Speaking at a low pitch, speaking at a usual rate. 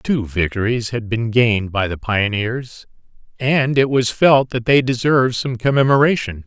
Yes: low, 120 Hz; average, 160 wpm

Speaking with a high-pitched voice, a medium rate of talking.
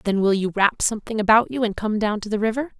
No: high, 215 Hz; fast, 280 wpm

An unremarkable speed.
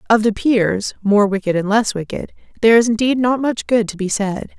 No: fast, 225 wpm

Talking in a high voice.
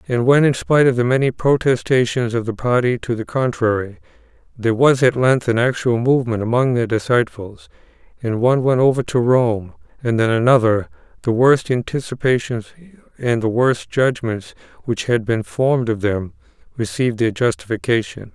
No: low, 120 Hz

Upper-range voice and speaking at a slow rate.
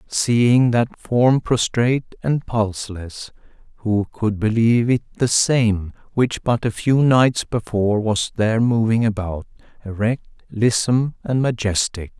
No: low, 115 Hz; slow, 130 wpm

